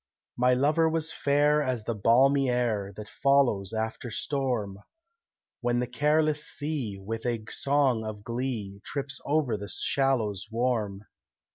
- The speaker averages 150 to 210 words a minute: No, slow, 135 wpm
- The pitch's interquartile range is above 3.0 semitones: Yes, average, 4.5 semitones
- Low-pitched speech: Yes, low, 125 Hz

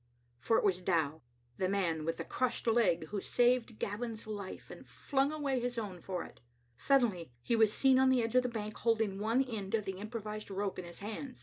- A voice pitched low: No, high, 215 Hz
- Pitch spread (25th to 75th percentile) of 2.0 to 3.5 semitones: No, average, 4.1 semitones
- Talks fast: Yes, fast, 220 wpm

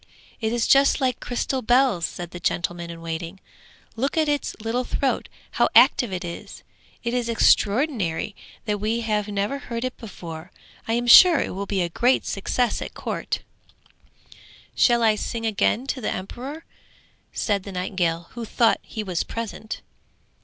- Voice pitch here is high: Yes, high, 220 Hz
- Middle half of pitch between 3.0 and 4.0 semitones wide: No, average, 4.7 semitones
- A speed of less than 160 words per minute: No, average, 165 wpm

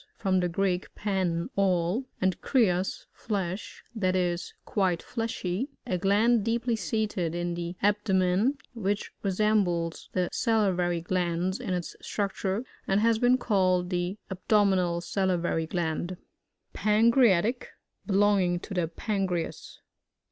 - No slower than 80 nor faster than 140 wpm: Yes, slow, 135 wpm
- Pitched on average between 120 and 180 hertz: No, high, 190 Hz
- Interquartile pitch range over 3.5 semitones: No, average, 3.1 semitones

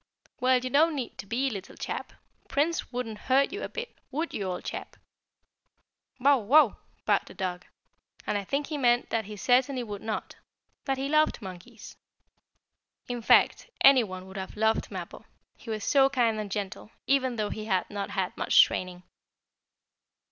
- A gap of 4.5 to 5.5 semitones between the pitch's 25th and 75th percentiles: Yes, average, 5.0 semitones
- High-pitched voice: Yes, high, 235 Hz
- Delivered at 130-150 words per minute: No, average, 175 wpm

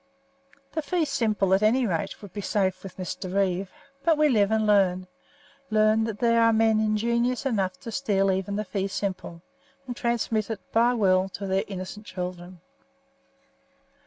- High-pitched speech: Yes, high, 210 Hz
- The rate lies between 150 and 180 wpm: Yes, average, 165 wpm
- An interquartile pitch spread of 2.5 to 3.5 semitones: Yes, average, 3.2 semitones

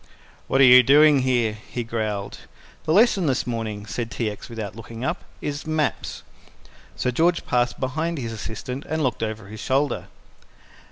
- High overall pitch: No, low, 125 Hz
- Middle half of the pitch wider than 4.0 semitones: Yes, average, 4.4 semitones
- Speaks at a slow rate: No, average, 165 wpm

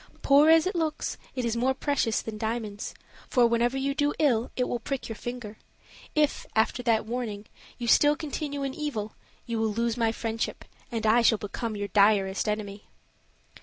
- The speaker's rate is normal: Yes, average, 180 wpm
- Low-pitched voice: No, high, 235 Hz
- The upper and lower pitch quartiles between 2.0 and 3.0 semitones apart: No, average, 3.9 semitones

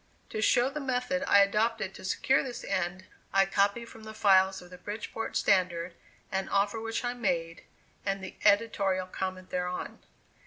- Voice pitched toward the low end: No, high, 200 Hz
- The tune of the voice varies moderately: Yes, average, 3.3 semitones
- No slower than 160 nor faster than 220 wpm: Yes, average, 165 wpm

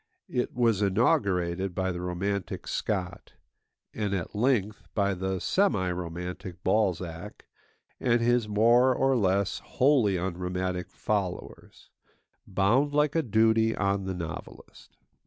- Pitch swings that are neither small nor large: Yes, average, 3.9 semitones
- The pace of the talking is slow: Yes, slow, 120 wpm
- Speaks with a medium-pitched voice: No, low, 100 Hz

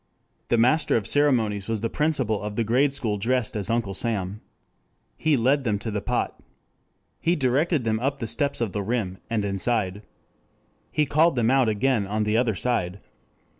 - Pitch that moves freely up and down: No, average, 4.3 semitones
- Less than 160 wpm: No, average, 180 wpm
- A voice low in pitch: Yes, low, 115 Hz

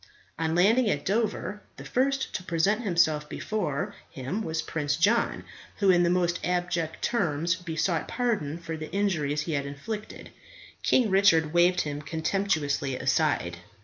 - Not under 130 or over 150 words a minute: Yes, average, 145 wpm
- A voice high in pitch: No, medium, 170 Hz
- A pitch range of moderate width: Yes, average, 4.8 semitones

